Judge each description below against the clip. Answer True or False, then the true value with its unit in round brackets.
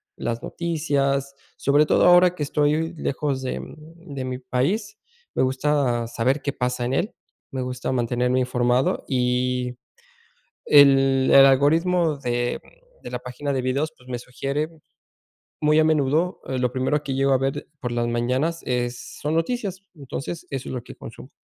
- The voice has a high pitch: False (135 Hz)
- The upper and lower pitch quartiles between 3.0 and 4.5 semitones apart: True (3.3 semitones)